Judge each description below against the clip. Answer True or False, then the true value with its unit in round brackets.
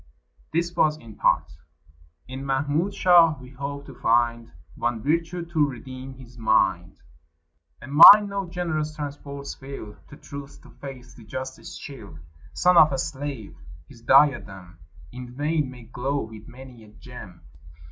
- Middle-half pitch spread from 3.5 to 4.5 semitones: True (4.0 semitones)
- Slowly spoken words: False (145 wpm)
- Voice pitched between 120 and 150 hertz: True (135 Hz)